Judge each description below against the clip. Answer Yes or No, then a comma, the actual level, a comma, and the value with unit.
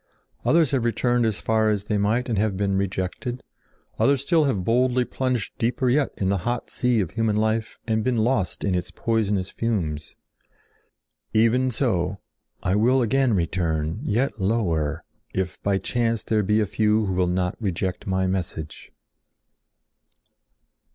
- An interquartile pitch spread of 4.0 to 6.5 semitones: Yes, average, 4.3 semitones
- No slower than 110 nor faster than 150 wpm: No, average, 160 wpm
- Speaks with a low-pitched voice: Yes, low, 110 Hz